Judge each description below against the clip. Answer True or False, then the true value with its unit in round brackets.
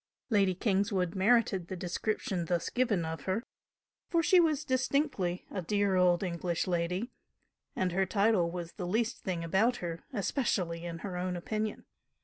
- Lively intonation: False (3.8 semitones)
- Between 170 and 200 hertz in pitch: True (190 Hz)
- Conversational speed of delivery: True (155 wpm)